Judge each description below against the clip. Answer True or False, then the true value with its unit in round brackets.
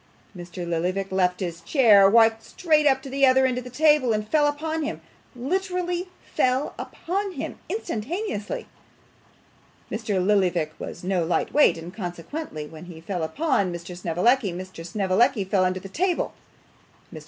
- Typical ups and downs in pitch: False (8.4 semitones)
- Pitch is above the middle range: True (210 Hz)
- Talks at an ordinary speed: True (155 wpm)